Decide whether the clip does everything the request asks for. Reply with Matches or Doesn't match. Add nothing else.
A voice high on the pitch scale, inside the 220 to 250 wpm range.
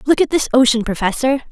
Doesn't match